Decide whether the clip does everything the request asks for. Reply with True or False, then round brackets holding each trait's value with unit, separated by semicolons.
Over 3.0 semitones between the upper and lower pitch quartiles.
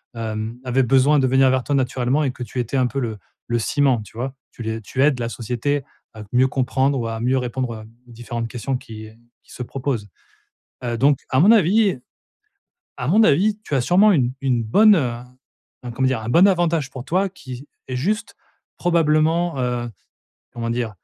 True (3.7 semitones)